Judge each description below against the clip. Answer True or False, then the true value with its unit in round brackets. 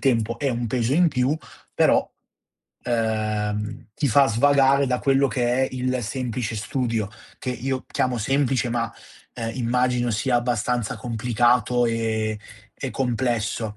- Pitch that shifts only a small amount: True (2.3 semitones)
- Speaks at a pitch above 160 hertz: False (120 Hz)